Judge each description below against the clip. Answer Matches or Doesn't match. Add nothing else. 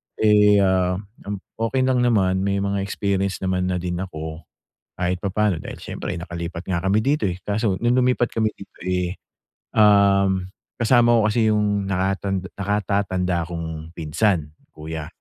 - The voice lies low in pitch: Matches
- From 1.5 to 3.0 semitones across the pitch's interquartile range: Matches